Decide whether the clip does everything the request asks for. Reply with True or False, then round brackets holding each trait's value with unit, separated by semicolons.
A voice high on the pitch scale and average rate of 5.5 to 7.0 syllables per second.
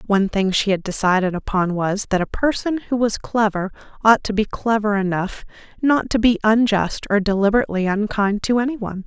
True (210 Hz; 5.6 syllables/s)